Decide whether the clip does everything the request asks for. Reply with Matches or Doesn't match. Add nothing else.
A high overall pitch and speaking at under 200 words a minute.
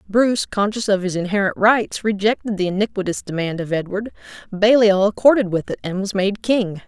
Matches